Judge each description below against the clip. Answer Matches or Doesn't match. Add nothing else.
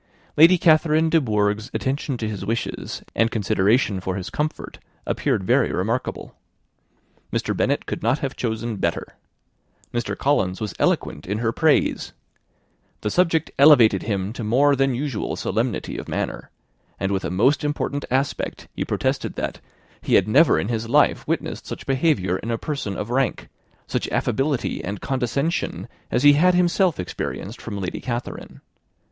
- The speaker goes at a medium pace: Matches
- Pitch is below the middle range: Matches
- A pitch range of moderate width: Doesn't match